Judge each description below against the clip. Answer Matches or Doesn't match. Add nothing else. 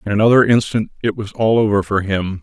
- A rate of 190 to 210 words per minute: Doesn't match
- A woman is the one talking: Doesn't match